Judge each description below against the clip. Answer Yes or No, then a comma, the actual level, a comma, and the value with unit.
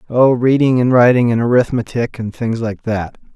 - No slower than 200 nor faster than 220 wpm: No, average, 180 wpm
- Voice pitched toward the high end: No, low, 120 Hz